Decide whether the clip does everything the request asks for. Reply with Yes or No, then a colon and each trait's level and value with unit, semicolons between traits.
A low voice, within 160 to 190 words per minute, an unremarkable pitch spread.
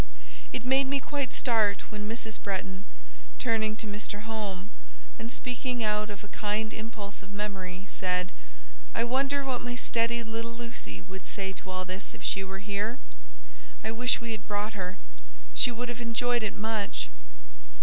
No: high, 215 Hz; average, 165 wpm; average, 3.3 semitones